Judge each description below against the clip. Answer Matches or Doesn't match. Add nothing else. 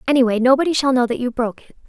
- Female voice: Matches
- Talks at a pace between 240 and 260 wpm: Matches